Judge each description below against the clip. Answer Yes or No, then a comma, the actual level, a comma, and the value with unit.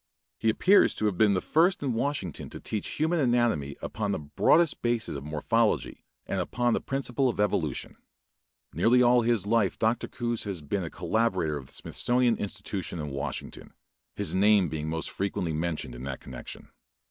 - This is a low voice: Yes, low, 105 Hz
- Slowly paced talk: No, average, 175 wpm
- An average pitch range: No, wide, 6.8 semitones